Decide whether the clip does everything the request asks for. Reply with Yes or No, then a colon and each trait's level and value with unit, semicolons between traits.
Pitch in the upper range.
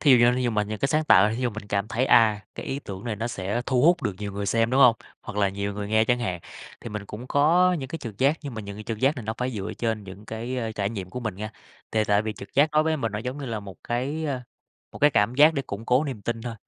No: low, 115 Hz